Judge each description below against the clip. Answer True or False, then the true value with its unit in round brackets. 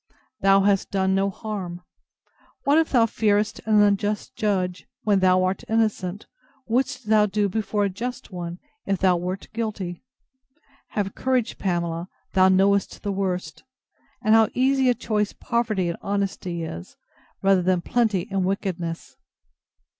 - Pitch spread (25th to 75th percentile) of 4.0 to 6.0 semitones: False (2.8 semitones)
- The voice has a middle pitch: False (195 Hz)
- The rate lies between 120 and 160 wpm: True (145 wpm)